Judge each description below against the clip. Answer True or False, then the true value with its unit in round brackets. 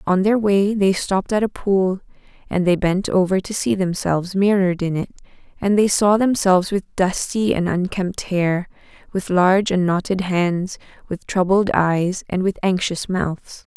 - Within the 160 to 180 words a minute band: True (170 wpm)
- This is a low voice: False (190 Hz)